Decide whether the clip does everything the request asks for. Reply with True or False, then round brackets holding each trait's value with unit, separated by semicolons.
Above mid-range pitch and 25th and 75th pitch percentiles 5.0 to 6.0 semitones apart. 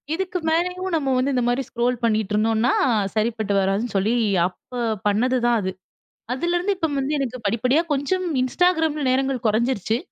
True (255 Hz; 5.4 semitones)